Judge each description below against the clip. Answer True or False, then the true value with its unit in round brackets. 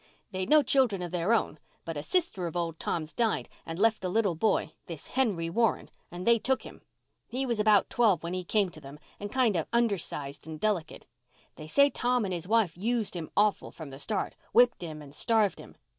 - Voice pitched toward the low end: False (195 Hz)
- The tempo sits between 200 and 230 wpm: True (205 wpm)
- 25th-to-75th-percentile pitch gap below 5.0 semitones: False (5.6 semitones)